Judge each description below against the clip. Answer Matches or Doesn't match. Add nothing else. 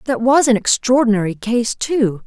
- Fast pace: Doesn't match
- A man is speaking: Doesn't match